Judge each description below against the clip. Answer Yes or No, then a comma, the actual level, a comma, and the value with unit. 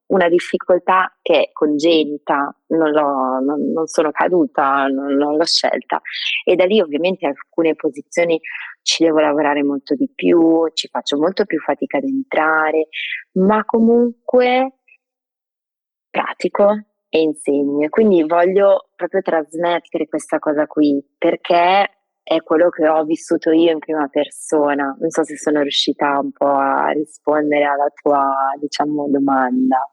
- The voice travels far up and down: No, average, 3.3 semitones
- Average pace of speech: Yes, average, 140 wpm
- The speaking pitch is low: No, medium, 155 Hz